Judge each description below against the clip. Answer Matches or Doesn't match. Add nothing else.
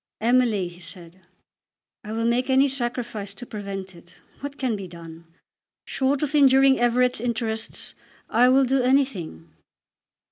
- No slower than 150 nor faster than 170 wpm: Doesn't match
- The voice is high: Matches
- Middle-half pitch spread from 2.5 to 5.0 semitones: Doesn't match